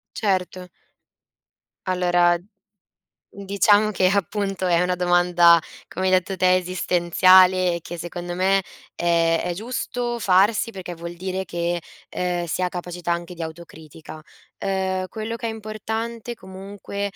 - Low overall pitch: No, medium, 185 Hz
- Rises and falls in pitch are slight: Yes, narrow, 2.3 semitones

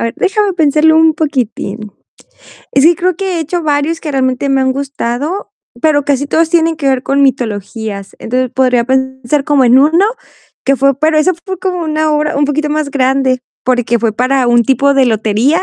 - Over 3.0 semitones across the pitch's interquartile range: Yes, average, 3.6 semitones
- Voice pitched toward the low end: No, very high, 275 Hz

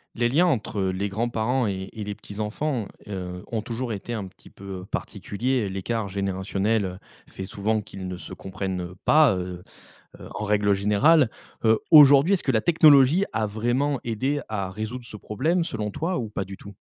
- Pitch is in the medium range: No, low, 110 Hz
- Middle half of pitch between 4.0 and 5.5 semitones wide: Yes, average, 4.6 semitones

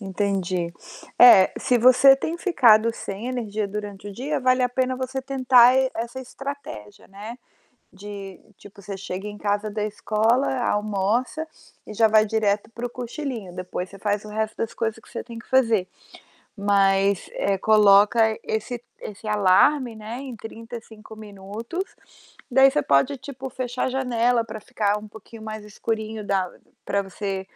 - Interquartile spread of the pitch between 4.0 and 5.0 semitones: No, average, 3.5 semitones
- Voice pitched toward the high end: Yes, high, 220 Hz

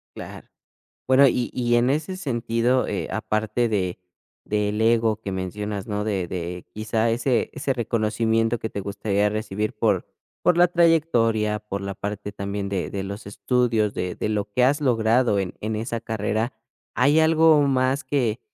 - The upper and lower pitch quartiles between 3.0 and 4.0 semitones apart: Yes, average, 3.4 semitones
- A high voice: No, low, 110 Hz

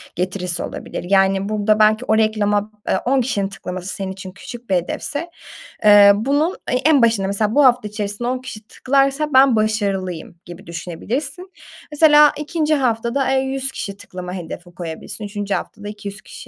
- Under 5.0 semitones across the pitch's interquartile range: No, average, 5.3 semitones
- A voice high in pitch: Yes, high, 215 Hz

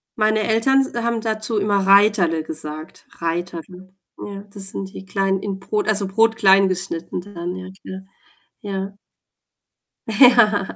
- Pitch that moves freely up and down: No, narrow, 2.5 semitones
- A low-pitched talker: No, high, 195 Hz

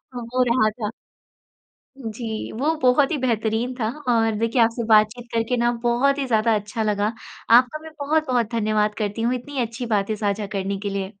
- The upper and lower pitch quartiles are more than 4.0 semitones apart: No, average, 2.7 semitones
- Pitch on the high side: Yes, high, 230 Hz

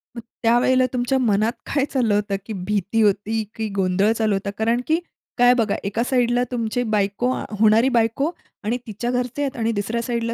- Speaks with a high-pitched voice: Yes, high, 230 Hz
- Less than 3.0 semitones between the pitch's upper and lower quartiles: Yes, narrow, 2.6 semitones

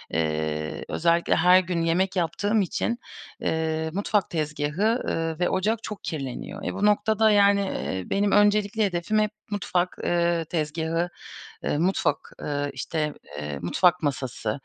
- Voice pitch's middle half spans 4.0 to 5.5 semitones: Yes, average, 4.9 semitones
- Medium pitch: Yes, medium, 175 Hz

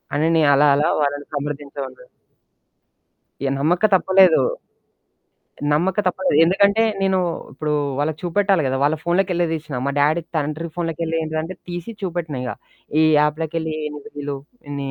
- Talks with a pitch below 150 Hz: No, medium, 160 Hz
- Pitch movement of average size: Yes, average, 3.2 semitones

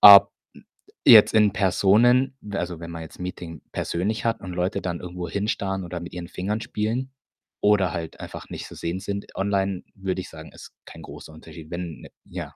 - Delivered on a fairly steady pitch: No, average, 3.0 semitones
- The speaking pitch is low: Yes, very low, 95 Hz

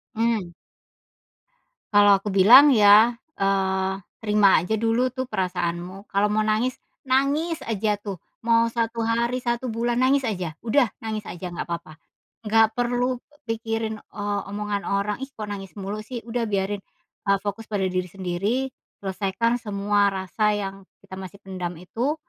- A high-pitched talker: Yes, high, 210 Hz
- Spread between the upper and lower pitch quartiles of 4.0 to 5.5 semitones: No, average, 3.1 semitones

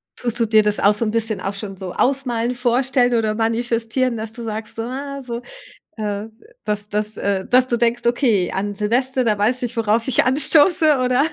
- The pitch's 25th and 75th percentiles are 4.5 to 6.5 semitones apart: No, average, 2.9 semitones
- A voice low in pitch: No, high, 230 Hz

